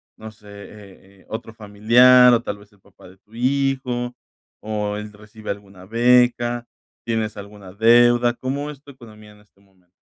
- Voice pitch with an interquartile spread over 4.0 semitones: No, average, 2.9 semitones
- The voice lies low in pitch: Yes, low, 110 Hz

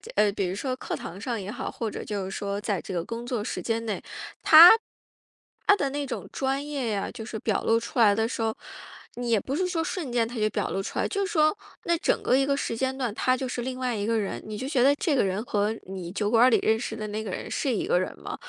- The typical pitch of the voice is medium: No, high, 230 Hz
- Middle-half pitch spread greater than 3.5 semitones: Yes, average, 4.3 semitones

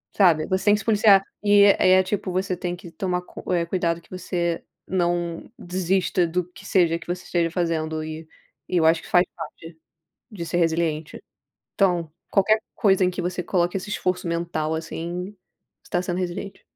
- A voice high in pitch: No, medium, 175 Hz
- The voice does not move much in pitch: Yes, narrow, 1.9 semitones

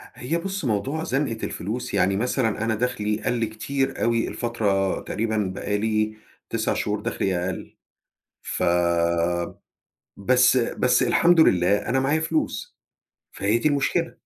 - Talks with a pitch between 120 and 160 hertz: No, low, 110 Hz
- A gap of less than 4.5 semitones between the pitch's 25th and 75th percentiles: No, average, 5.3 semitones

